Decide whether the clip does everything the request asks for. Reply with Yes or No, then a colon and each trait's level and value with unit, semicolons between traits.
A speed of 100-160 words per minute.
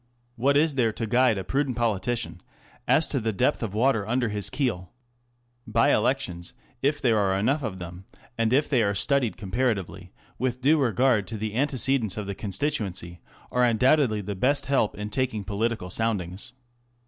No: average, 170 wpm